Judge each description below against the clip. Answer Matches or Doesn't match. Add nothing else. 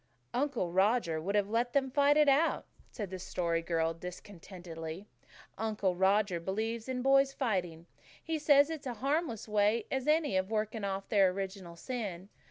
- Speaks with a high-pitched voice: Matches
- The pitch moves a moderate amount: Doesn't match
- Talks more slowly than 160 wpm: Doesn't match